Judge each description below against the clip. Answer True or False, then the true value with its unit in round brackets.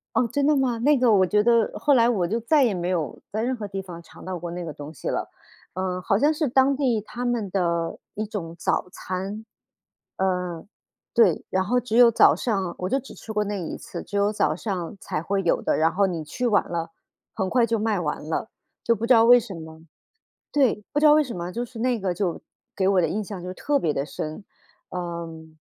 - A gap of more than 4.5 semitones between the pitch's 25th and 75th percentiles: True (5.2 semitones)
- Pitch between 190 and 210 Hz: True (200 Hz)